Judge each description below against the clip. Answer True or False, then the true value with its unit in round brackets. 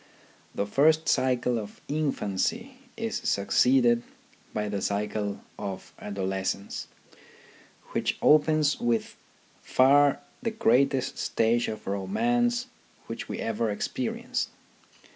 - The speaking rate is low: True (105 wpm)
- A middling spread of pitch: False (6.9 semitones)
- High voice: False (120 Hz)